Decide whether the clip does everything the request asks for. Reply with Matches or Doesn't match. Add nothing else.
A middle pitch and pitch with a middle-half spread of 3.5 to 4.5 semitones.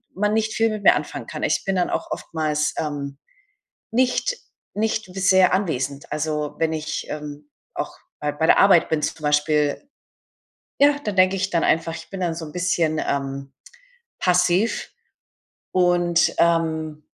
Matches